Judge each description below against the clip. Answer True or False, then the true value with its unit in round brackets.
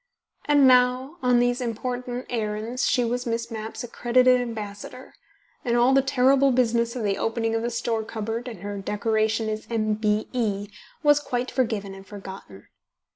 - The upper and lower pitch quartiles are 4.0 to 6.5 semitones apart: False (2.5 semitones)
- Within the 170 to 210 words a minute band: False (155 wpm)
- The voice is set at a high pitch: True (235 Hz)